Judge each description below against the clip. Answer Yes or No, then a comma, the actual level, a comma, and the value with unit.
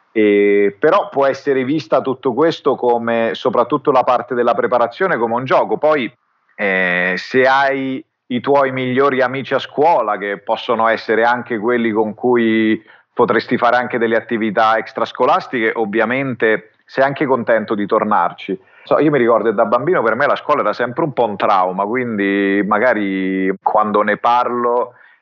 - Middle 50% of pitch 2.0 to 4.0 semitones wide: Yes, average, 3.3 semitones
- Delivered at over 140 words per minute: Yes, average, 155 wpm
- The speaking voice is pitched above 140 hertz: No, low, 120 Hz